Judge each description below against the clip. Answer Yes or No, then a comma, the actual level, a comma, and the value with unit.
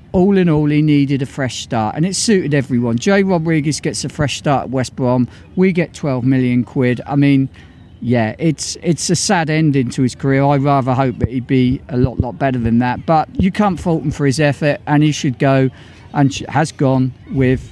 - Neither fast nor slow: No, fast, 220 wpm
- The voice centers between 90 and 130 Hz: No, medium, 140 Hz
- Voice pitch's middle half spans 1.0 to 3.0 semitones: No, average, 3.4 semitones